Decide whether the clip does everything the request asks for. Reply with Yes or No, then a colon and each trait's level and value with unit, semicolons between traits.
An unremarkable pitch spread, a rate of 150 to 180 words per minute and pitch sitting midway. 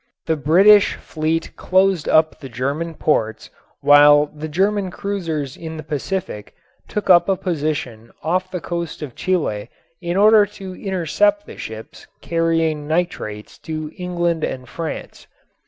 No: average, 3.8 semitones; average, 140 wpm; medium, 165 Hz